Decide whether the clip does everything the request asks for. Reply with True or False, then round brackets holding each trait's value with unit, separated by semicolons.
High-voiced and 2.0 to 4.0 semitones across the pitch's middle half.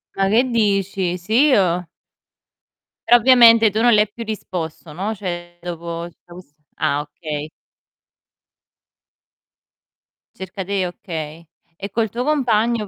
False (195 Hz; 4.4 semitones)